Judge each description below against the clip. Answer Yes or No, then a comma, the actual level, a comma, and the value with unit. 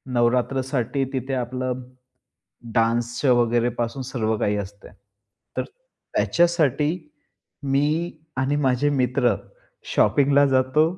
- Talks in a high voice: No, low, 130 Hz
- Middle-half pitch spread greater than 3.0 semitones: No, average, 2.7 semitones